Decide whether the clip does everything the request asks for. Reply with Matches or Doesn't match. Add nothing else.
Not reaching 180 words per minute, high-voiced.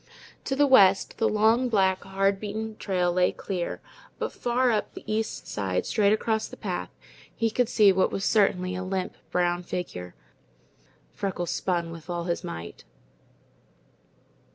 Matches